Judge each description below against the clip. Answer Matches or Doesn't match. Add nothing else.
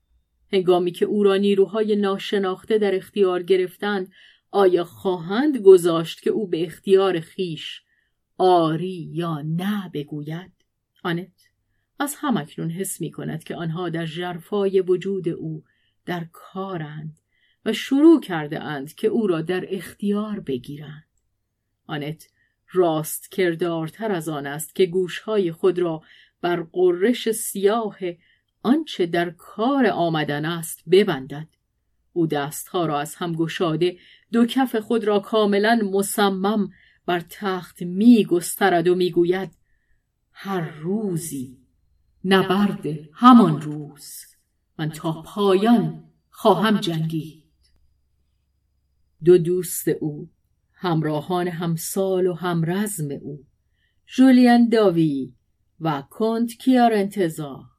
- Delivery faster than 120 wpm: Doesn't match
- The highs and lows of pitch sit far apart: Doesn't match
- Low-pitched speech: Doesn't match